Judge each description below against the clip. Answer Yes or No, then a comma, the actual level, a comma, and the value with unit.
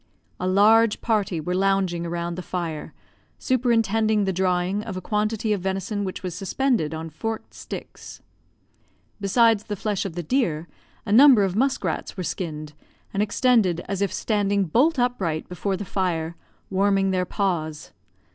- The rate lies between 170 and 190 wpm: No, average, 155 wpm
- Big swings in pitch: No, average, 3.5 semitones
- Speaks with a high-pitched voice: Yes, high, 195 Hz